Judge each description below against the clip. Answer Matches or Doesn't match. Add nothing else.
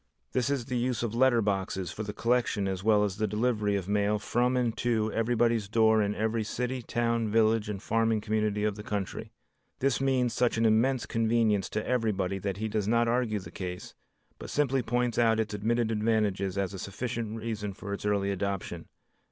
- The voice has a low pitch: Matches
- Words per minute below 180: Doesn't match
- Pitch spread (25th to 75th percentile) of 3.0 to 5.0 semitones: Doesn't match